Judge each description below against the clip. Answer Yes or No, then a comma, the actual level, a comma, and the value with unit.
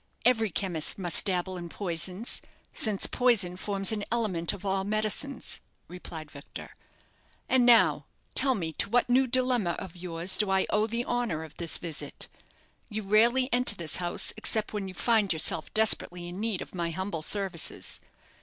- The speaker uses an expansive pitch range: No, average, 4.4 semitones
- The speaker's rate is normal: Yes, average, 165 wpm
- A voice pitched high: Yes, high, 195 Hz